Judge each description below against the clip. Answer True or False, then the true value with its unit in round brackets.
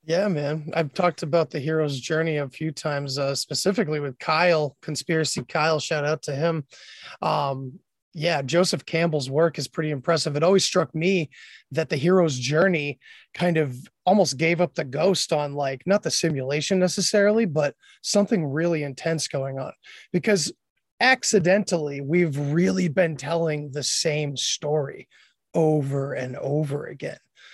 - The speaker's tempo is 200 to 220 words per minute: False (150 wpm)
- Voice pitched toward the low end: False (160 Hz)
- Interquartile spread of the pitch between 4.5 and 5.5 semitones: False (3.3 semitones)